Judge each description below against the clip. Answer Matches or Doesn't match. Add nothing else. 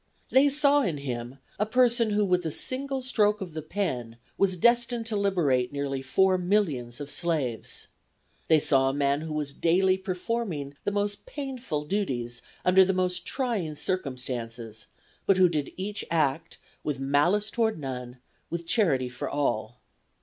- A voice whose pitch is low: Doesn't match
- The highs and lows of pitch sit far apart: Matches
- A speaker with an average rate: Matches